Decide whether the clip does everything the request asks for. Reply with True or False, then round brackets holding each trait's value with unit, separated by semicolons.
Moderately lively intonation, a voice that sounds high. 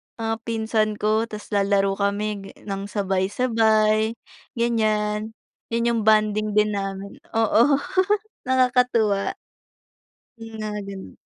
False (1.9 semitones; 215 Hz)